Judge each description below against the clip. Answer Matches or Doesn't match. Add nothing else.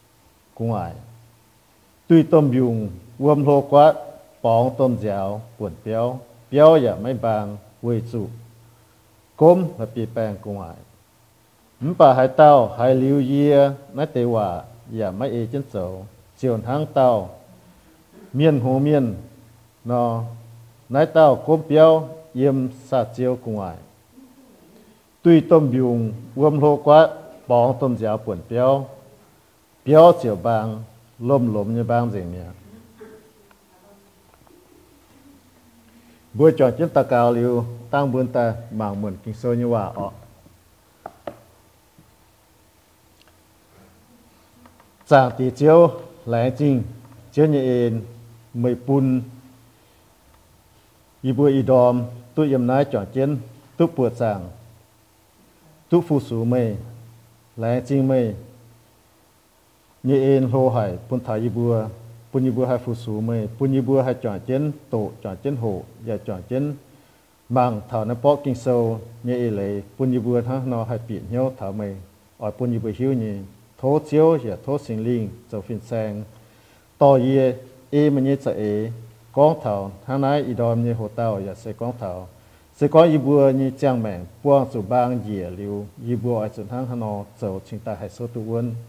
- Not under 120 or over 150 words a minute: Matches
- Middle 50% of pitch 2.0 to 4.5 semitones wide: Matches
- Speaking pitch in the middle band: Doesn't match